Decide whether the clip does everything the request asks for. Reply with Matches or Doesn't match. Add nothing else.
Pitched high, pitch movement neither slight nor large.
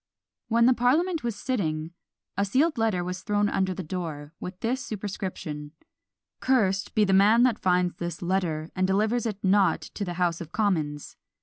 Matches